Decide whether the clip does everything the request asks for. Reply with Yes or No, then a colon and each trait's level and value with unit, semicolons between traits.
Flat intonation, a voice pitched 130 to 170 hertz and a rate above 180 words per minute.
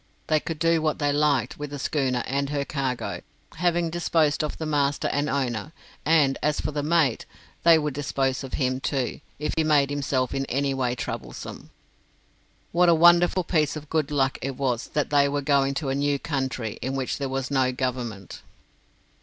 Yes: narrow, 2.3 semitones; medium, 140 Hz; average, 190 wpm